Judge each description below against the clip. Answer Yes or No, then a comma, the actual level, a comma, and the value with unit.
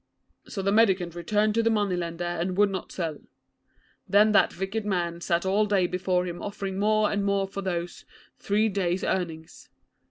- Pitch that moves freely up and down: No, average, 2.9 semitones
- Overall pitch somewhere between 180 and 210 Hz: Yes, high, 190 Hz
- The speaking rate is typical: Yes, average, 180 wpm